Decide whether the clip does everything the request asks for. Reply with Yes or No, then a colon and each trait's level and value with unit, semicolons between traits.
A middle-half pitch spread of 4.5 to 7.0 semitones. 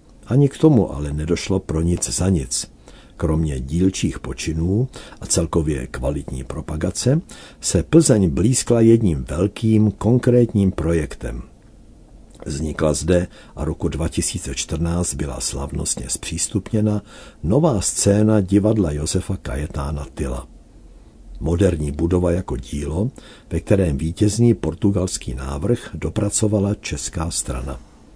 Yes: wide, 5.5 semitones